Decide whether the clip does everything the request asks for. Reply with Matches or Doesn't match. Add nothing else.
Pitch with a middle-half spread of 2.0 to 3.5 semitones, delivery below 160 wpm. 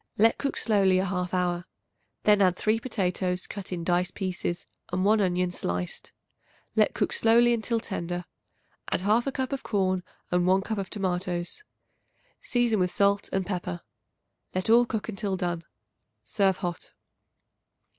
Matches